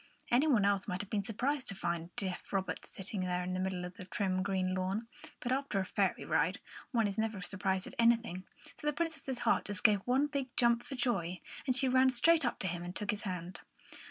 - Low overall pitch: No, high, 205 Hz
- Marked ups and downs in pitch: No, average, 5.0 semitones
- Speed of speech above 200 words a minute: Yes, fast, 230 wpm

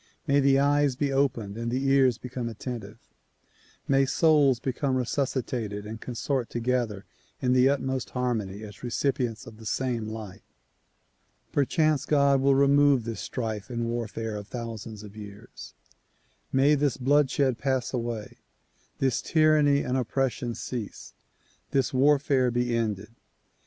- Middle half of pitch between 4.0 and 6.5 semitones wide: No, average, 3.3 semitones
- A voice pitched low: Yes, low, 125 Hz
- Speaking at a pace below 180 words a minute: Yes, slow, 135 wpm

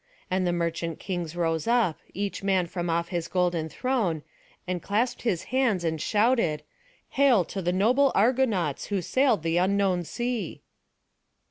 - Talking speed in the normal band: Yes, average, 150 wpm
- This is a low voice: No, medium, 185 Hz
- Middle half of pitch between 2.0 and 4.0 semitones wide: No, average, 5.2 semitones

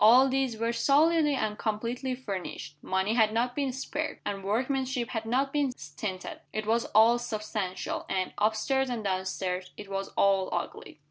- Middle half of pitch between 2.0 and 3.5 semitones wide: No, average, 4.8 semitones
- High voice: Yes, high, 225 Hz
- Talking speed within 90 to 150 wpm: No, average, 175 wpm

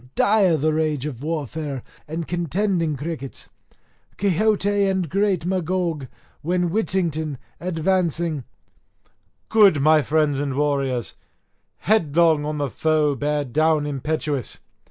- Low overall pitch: No, medium, 160 Hz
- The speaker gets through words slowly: Yes, slow, 110 wpm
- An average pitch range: Yes, average, 3.5 semitones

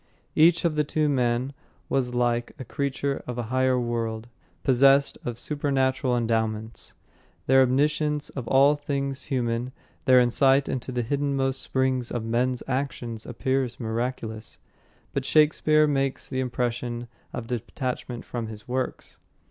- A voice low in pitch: Yes, low, 130 Hz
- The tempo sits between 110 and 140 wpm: Yes, slow, 135 wpm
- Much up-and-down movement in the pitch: No, narrow, 2.4 semitones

